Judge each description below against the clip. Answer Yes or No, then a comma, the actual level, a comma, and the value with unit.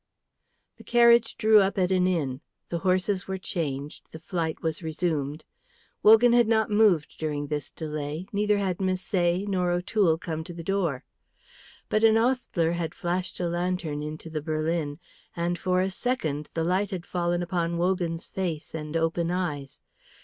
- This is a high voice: No, medium, 175 Hz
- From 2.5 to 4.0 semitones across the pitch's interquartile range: Yes, average, 3.1 semitones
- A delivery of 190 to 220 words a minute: No, average, 165 wpm